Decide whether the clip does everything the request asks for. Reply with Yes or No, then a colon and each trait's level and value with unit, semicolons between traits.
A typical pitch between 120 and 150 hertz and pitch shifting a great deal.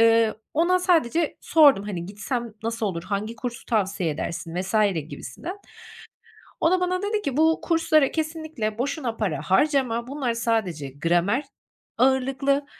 No: high, 235 Hz; wide, 7.2 semitones